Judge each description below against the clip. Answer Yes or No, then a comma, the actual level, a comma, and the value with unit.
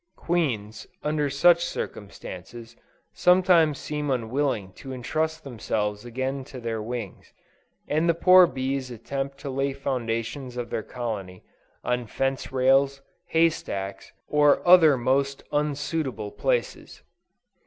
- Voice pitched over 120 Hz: Yes, low, 135 Hz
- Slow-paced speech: Yes, slow, 120 wpm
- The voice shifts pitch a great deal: No, average, 4.1 semitones